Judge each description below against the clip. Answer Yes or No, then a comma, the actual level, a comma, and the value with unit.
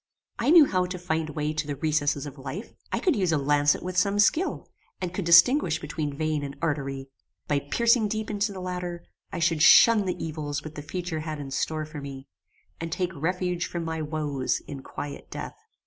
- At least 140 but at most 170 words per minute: No, fast, 205 wpm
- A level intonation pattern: No, average, 3.8 semitones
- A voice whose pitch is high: No, medium, 160 Hz